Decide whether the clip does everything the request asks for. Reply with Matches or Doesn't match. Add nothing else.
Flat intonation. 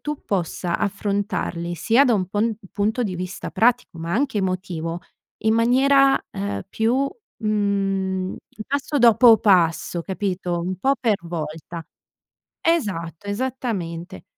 Doesn't match